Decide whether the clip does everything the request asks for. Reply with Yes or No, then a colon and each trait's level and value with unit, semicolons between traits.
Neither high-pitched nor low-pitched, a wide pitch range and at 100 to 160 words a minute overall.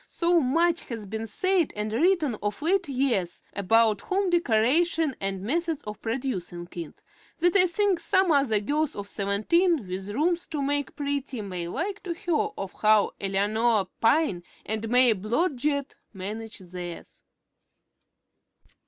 No: very high, 250 Hz; wide, 8.3 semitones; average, 145 wpm